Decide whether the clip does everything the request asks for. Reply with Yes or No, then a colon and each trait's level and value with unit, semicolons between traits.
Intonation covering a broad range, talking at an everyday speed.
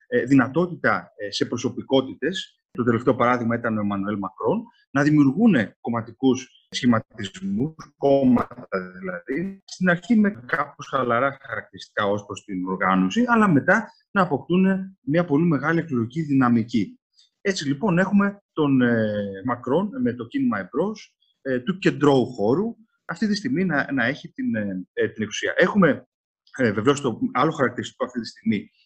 Yes: wide, 8.4 semitones; average, 135 wpm